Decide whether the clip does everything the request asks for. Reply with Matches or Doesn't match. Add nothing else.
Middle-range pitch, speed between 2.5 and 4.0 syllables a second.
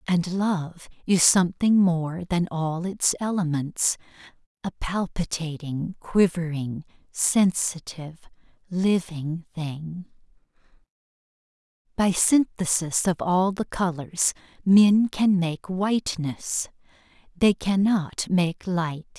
Matches